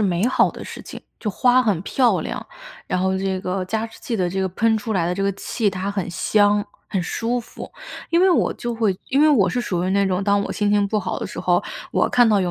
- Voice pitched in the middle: No, high, 205 Hz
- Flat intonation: No, average, 3.3 semitones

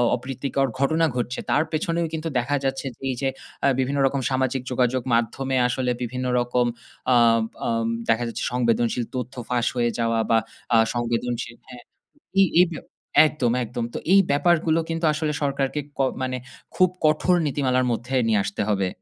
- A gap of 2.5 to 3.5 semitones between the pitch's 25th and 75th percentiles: Yes, average, 3.0 semitones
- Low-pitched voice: Yes, low, 130 Hz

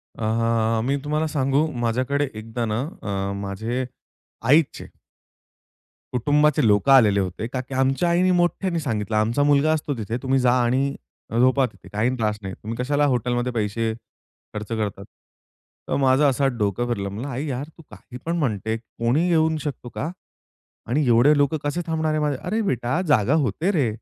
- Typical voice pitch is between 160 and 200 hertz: No, low, 130 Hz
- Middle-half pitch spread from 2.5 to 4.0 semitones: No, average, 4.6 semitones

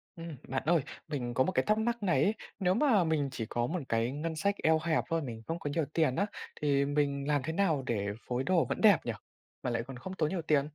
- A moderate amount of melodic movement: Yes, average, 4.4 semitones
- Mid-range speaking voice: Yes, medium, 155 Hz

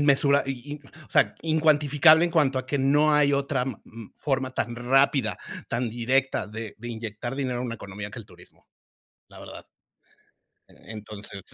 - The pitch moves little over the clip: No, average, 3.8 semitones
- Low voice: Yes, low, 130 Hz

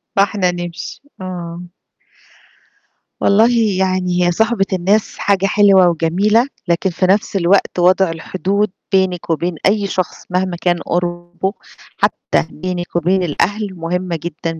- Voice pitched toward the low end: No, medium, 185 Hz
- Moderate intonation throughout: No, narrow, 2.1 semitones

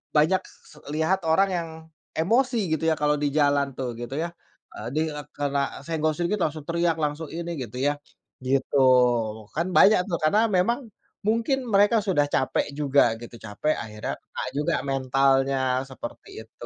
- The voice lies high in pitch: No, medium, 155 Hz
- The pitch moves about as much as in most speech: Yes, average, 4.5 semitones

